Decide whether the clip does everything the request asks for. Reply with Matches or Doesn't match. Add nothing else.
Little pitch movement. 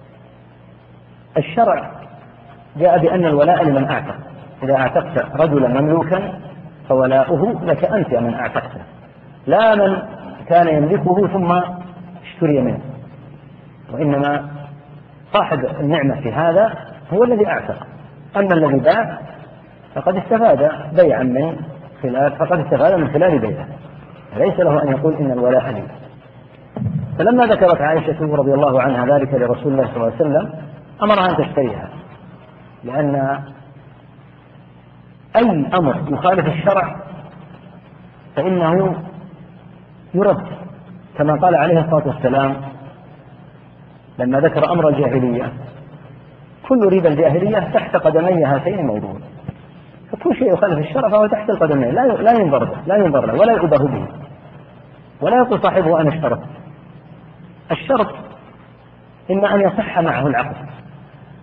Doesn't match